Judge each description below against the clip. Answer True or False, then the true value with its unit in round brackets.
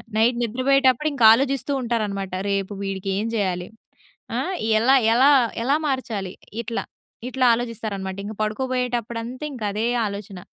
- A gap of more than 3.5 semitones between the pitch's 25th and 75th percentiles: True (4.2 semitones)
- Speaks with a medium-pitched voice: False (230 Hz)